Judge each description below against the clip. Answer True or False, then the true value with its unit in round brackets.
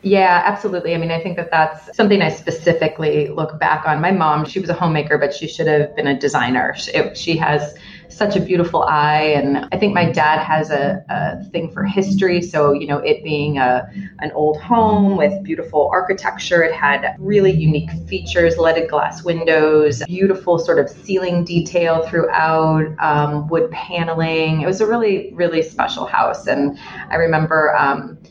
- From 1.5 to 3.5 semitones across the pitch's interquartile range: True (3.1 semitones)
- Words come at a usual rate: True (180 wpm)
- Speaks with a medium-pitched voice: True (165 Hz)